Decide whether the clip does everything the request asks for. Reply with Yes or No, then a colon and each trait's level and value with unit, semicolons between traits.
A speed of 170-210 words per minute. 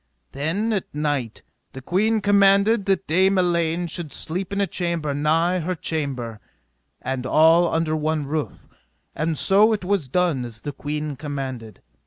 No: average, 155 wpm